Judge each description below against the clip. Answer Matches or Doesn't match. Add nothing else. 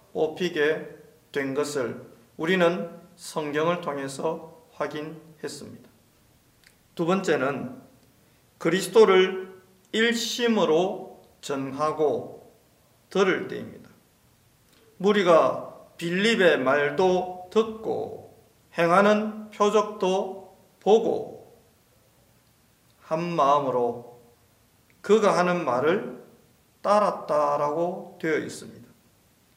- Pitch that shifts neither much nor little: Matches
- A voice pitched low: Doesn't match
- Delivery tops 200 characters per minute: Doesn't match